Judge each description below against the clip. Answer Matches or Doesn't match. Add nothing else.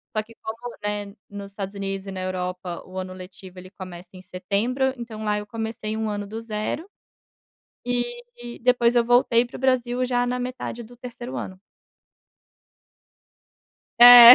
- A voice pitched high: Matches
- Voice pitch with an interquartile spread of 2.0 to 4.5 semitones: Matches